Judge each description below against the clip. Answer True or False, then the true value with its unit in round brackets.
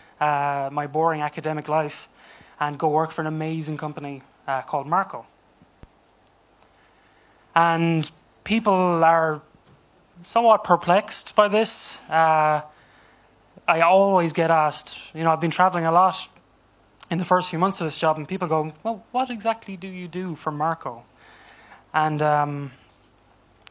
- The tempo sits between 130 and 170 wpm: True (140 wpm)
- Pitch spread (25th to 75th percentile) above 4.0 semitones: False (3.3 semitones)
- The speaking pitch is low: False (160 Hz)